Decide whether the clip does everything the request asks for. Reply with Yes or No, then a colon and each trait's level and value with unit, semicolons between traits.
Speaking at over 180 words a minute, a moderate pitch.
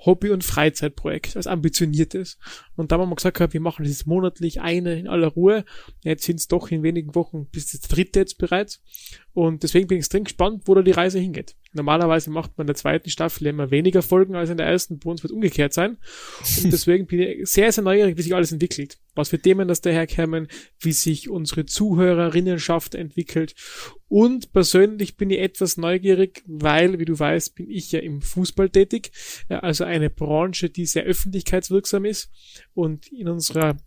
Yes: fast, 190 wpm; medium, 175 Hz